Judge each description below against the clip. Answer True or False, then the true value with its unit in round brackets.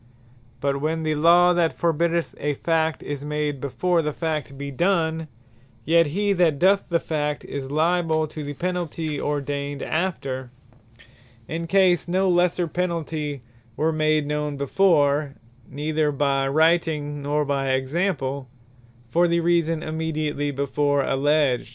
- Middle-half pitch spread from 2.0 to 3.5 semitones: True (2.9 semitones)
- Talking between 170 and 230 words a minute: False (135 wpm)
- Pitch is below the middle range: False (155 Hz)